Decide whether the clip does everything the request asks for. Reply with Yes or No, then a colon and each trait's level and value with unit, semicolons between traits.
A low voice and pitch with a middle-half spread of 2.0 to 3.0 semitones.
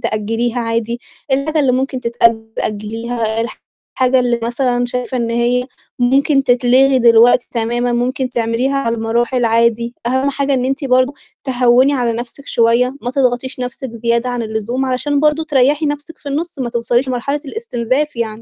No: high, 245 Hz; narrow, 2.4 semitones